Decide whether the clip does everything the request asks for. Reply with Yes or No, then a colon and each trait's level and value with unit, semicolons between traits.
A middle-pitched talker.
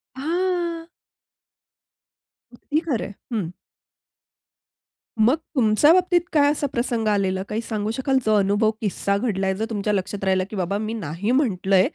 No: high, 215 Hz